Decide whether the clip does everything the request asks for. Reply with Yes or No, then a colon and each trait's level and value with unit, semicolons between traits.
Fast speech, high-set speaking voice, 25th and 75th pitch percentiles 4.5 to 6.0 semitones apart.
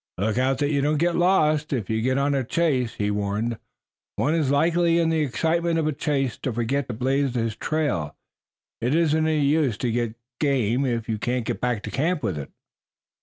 No: fast, 210 wpm; low, 135 Hz; average, 4.9 semitones